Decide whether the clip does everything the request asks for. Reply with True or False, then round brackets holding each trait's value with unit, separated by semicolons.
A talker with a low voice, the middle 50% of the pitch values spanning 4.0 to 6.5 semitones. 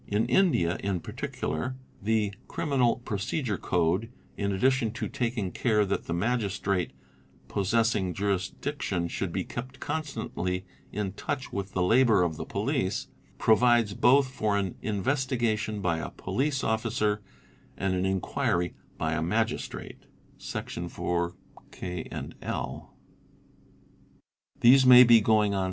True (105 Hz; 4.6 semitones)